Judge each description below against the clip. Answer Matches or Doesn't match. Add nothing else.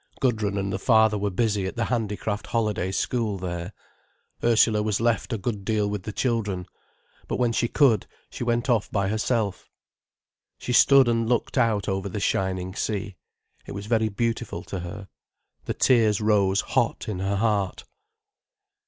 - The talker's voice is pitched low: Matches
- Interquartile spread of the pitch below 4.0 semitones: Matches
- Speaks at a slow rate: Doesn't match